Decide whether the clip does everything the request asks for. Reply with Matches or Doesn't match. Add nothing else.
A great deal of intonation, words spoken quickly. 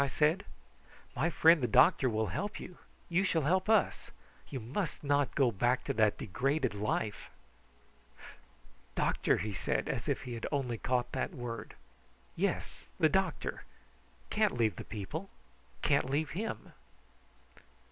Doesn't match